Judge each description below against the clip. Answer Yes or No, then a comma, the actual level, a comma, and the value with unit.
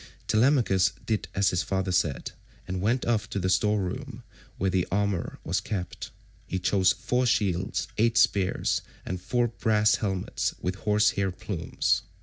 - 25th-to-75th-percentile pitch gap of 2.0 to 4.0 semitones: Yes, average, 2.7 semitones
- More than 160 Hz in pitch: No, low, 100 Hz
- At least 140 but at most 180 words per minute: Yes, average, 155 wpm